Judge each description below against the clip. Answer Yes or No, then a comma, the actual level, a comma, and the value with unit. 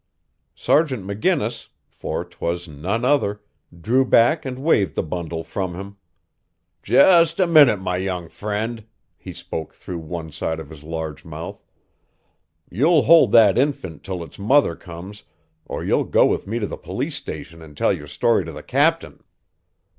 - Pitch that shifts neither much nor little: No, wide, 7.2 semitones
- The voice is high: No, low, 100 Hz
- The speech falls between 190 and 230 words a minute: No, average, 160 wpm